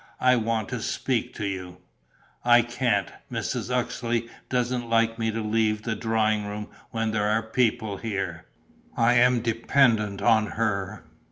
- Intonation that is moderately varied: No, narrow, 2.0 semitones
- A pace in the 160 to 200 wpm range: No, average, 150 wpm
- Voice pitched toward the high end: No, low, 115 Hz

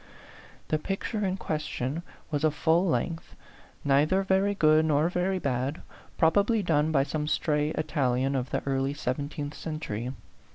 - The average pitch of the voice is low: No, medium, 155 Hz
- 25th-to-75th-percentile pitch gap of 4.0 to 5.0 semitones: No, average, 3.6 semitones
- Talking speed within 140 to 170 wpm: Yes, average, 150 wpm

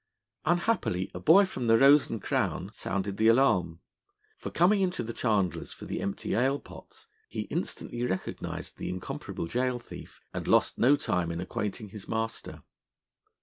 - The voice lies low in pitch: Yes, low, 115 Hz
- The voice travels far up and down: Yes, wide, 6.5 semitones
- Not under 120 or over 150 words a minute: No, average, 160 wpm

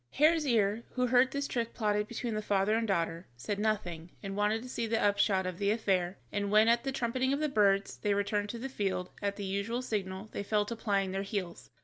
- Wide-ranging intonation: No, average, 2.9 semitones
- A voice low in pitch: No, high, 210 Hz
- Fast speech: Yes, fast, 235 wpm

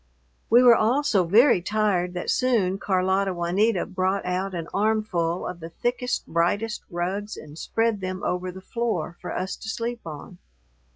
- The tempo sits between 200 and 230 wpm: No, average, 165 wpm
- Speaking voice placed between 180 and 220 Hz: Yes, high, 190 Hz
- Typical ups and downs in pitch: Yes, average, 3.7 semitones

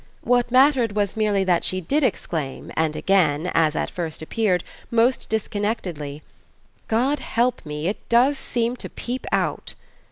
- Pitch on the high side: Yes, high, 205 Hz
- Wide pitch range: Yes, wide, 6.5 semitones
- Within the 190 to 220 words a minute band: No, average, 150 wpm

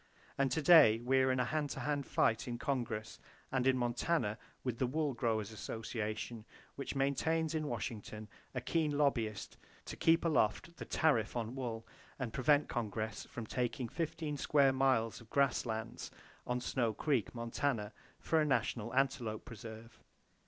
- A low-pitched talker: Yes, low, 125 Hz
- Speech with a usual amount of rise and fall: Yes, average, 4.1 semitones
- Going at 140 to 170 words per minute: Yes, average, 160 wpm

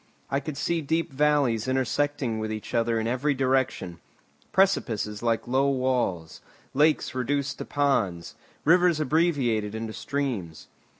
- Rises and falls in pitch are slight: No, average, 4.4 semitones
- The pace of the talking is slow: Yes, slow, 125 wpm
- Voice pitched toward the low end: Yes, low, 130 Hz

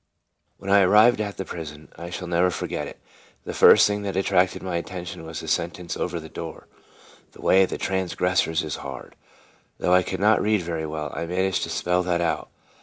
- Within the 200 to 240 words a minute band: Yes, fast, 205 wpm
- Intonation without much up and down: Yes, narrow, 2.3 semitones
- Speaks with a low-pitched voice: Yes, very low, 90 Hz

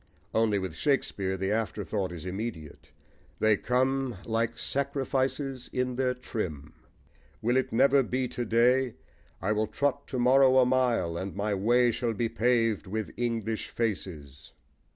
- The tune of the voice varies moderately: Yes, average, 3.9 semitones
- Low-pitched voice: Yes, low, 115 Hz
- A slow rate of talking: No, average, 145 wpm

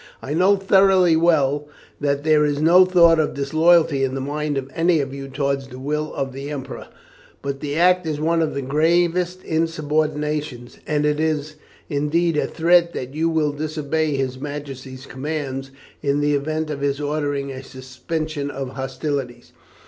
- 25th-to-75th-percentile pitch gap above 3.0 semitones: No, narrow, 2.6 semitones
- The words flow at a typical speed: Yes, average, 170 wpm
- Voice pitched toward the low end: No, medium, 150 Hz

